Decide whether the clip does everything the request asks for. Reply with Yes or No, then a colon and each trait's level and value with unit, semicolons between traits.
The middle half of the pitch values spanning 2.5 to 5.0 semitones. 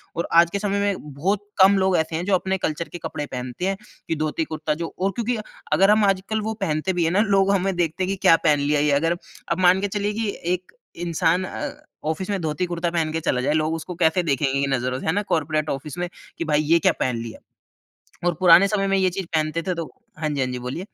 Yes: average, 3.8 semitones